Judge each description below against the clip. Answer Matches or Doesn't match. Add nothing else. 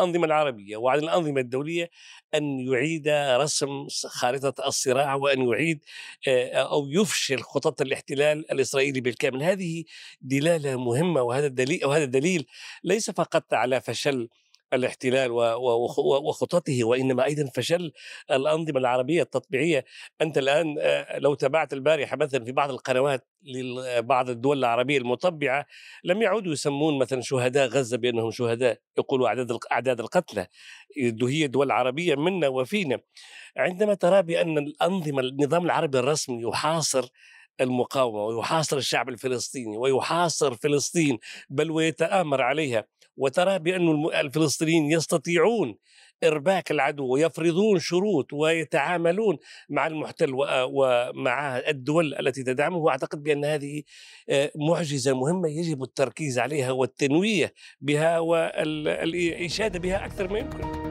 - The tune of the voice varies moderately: Matches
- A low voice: Doesn't match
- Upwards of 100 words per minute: Matches